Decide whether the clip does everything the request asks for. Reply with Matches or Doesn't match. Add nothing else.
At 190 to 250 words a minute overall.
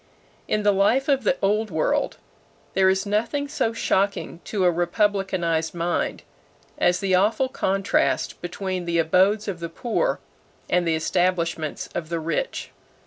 Doesn't match